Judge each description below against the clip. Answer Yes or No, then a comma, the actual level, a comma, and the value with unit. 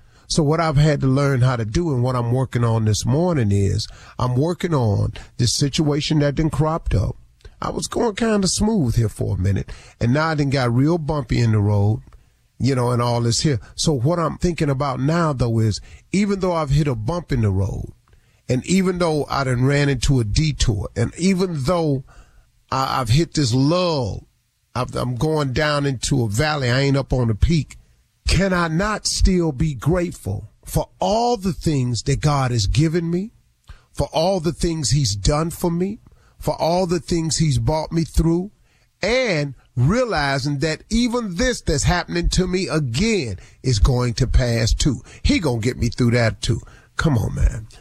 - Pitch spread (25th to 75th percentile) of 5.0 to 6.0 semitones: Yes, wide, 5.6 semitones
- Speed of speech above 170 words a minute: Yes, average, 190 wpm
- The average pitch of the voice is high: No, medium, 140 Hz